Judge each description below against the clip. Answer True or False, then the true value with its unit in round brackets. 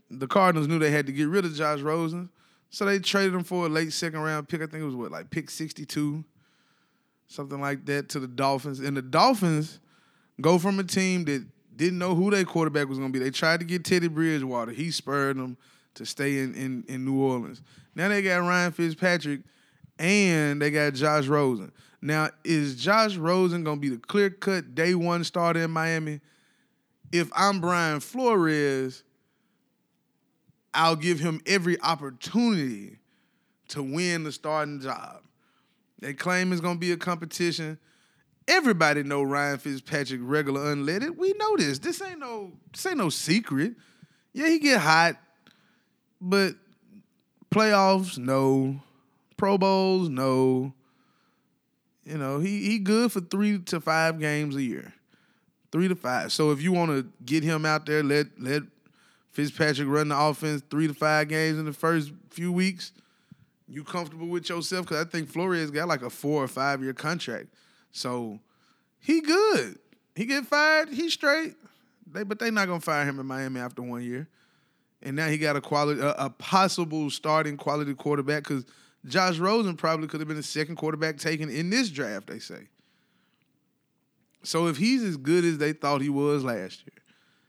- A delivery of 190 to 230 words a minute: False (175 wpm)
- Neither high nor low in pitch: True (160 Hz)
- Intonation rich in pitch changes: False (4.2 semitones)